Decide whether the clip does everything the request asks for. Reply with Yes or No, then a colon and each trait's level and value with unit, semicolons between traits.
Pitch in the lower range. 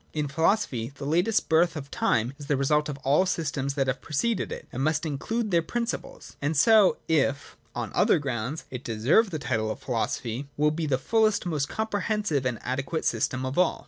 No: medium, 145 Hz